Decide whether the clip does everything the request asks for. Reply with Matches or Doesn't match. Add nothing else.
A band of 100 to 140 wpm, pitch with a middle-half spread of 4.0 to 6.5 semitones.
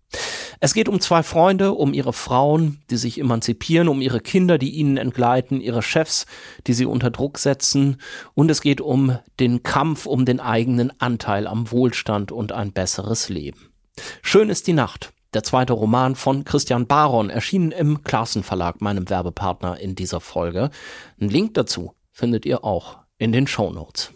Doesn't match